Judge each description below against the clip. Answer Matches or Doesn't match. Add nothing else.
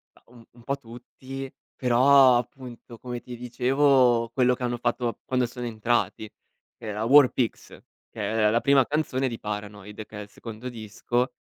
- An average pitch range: Doesn't match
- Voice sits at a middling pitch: Doesn't match